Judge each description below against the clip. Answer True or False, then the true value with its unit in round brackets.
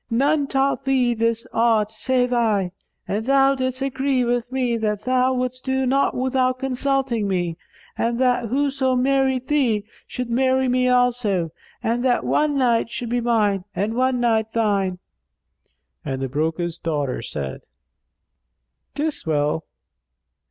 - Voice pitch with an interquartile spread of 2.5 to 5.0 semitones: True (3.4 semitones)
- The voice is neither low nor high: False (245 Hz)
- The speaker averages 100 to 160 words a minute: True (140 wpm)